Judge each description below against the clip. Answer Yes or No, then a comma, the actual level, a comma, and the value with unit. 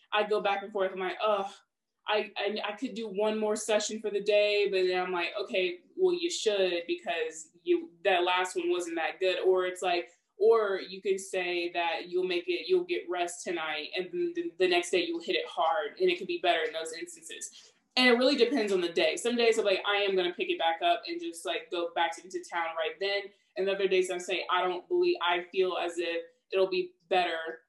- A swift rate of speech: Yes, fast, 240 wpm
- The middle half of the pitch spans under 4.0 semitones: No, average, 4.9 semitones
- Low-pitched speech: No, high, 195 Hz